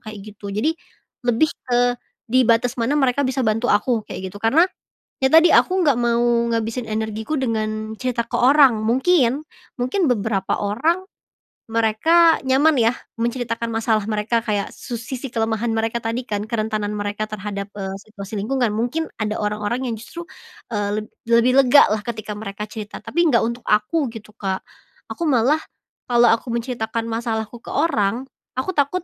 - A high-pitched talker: Yes, high, 230 Hz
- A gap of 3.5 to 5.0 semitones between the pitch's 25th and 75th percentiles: No, average, 3.1 semitones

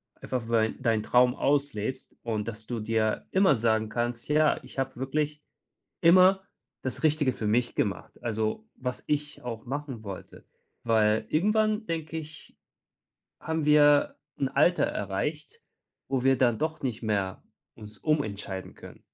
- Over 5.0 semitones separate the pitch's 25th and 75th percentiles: Yes, wide, 5.4 semitones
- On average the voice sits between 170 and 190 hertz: No, low, 130 Hz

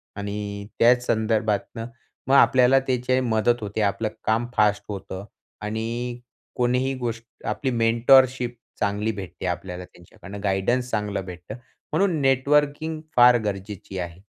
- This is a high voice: No, low, 115 Hz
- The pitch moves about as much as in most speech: Yes, average, 3.7 semitones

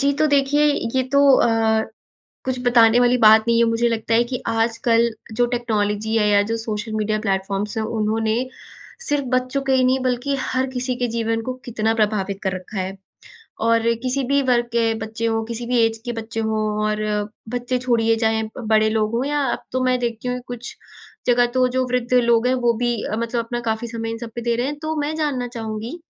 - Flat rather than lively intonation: Yes, narrow, 2.3 semitones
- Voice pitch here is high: Yes, high, 235 Hz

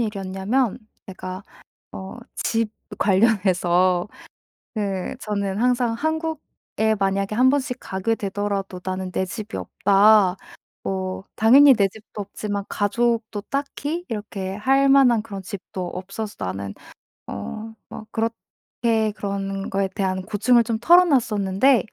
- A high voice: Yes, high, 205 Hz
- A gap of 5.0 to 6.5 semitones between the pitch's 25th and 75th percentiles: No, average, 3.4 semitones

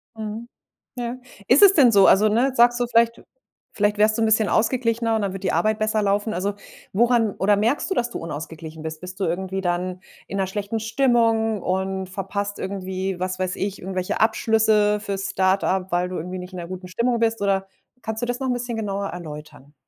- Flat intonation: No, average, 3.3 semitones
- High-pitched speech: Yes, high, 205 Hz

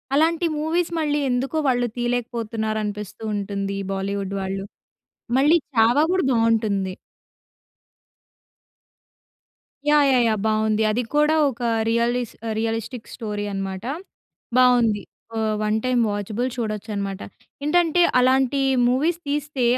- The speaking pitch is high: Yes, high, 230 Hz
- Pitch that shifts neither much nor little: Yes, average, 4.0 semitones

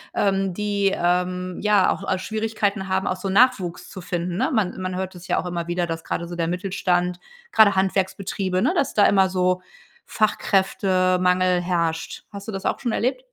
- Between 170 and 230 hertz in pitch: Yes, medium, 185 Hz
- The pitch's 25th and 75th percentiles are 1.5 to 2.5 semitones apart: Yes, narrow, 1.9 semitones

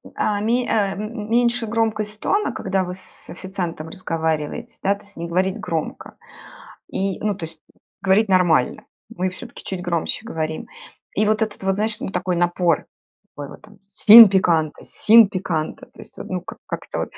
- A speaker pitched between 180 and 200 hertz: Yes, high, 190 Hz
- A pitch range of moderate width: Yes, average, 3.8 semitones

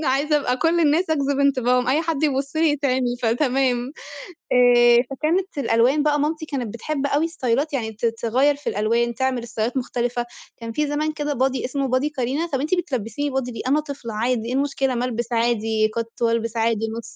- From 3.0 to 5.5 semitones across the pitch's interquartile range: Yes, average, 3.6 semitones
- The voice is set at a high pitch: Yes, very high, 260 Hz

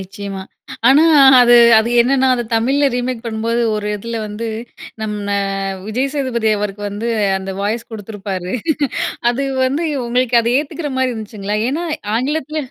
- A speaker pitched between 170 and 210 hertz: No, high, 235 Hz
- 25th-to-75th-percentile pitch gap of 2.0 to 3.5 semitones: No, average, 3.9 semitones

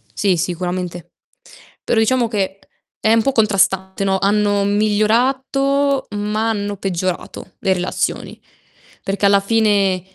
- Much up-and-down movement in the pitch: No, narrow, 2.6 semitones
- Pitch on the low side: No, high, 205 Hz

